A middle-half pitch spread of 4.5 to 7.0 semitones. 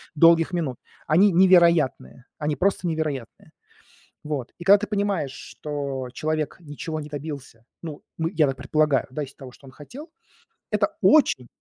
No: average, 3.5 semitones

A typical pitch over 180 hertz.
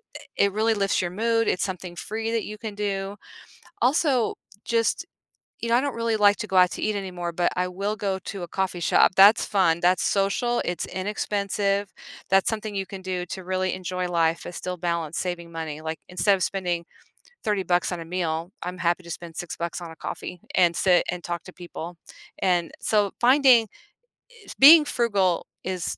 Yes: high, 190 Hz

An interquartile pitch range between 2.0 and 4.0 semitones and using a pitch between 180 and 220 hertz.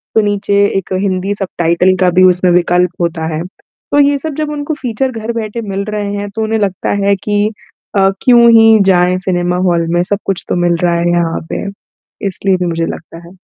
Yes: average, 3.1 semitones; high, 190 Hz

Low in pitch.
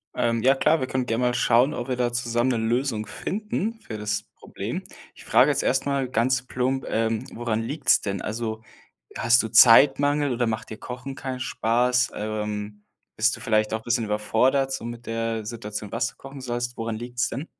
Yes: low, 120 Hz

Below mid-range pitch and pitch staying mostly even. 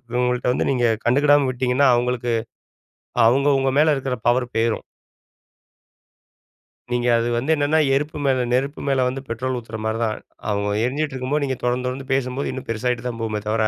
Yes: low, 125 Hz; narrow, 2.1 semitones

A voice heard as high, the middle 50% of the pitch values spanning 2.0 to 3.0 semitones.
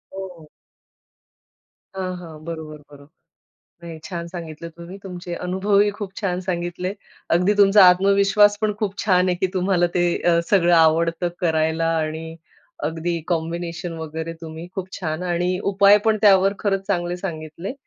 No: medium, 175 Hz; average, 2.7 semitones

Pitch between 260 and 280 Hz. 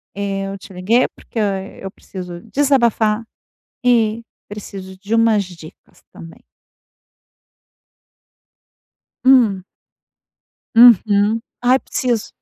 No: high, 210 Hz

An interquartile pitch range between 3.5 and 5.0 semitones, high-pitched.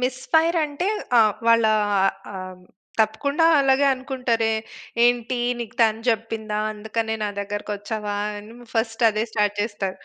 No: average, 3.1 semitones; high, 225 Hz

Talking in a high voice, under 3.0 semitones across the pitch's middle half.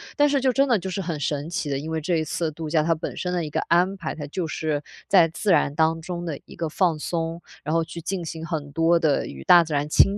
No: medium, 165 Hz; narrow, 2.4 semitones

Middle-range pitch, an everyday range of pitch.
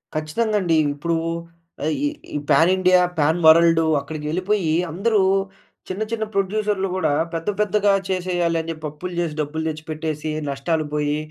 Yes: medium, 165 Hz; average, 3.4 semitones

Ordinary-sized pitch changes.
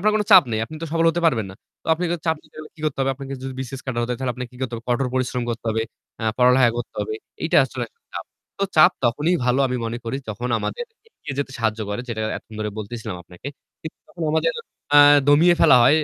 Yes: average, 4.8 semitones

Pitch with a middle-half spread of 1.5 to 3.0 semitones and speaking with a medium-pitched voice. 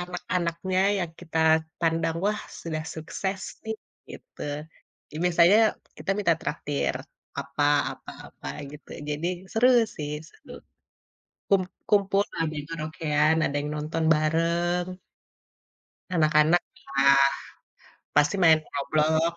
Yes: average, 2.7 semitones; medium, 165 Hz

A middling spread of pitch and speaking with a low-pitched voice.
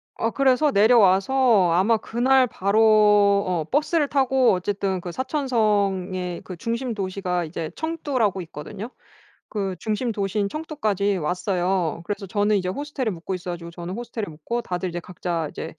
No: average, 4.7 semitones; high, 200 Hz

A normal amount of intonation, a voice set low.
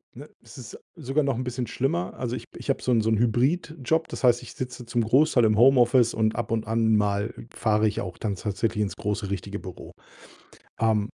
Yes: average, 3.1 semitones; low, 115 Hz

